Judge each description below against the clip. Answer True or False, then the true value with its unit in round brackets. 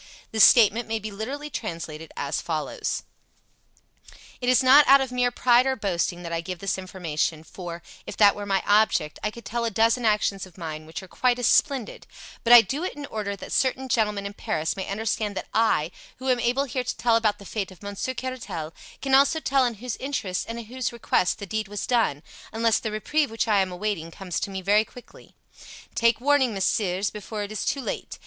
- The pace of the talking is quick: True (215 wpm)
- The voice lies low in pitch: False (215 Hz)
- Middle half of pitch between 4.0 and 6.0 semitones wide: True (4.4 semitones)